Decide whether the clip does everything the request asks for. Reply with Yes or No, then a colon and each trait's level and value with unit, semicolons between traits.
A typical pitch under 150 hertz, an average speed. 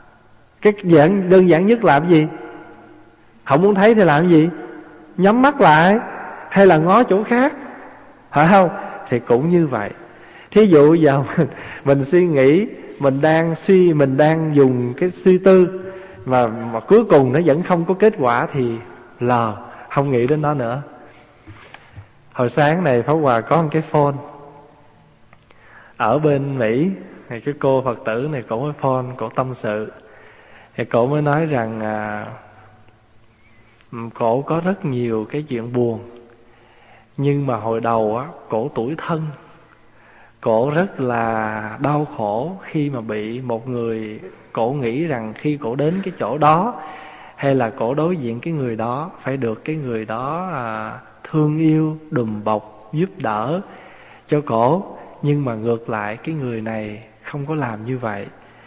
No: medium, 140 Hz; slow, 160 wpm